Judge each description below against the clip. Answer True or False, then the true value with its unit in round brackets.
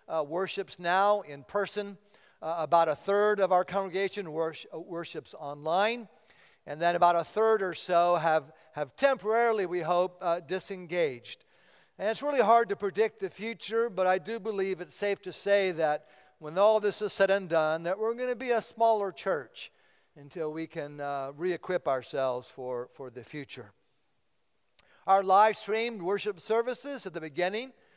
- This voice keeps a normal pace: True (170 wpm)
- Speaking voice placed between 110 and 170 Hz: False (185 Hz)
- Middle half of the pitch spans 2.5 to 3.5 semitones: False (4.5 semitones)